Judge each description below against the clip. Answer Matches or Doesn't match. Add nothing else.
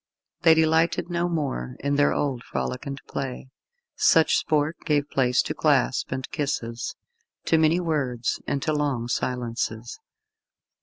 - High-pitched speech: Doesn't match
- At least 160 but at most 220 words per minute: Doesn't match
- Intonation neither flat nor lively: Matches